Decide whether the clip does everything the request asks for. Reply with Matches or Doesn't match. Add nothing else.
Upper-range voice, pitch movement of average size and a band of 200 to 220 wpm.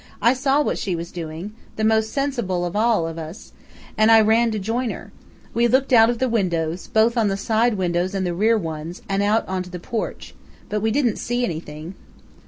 Matches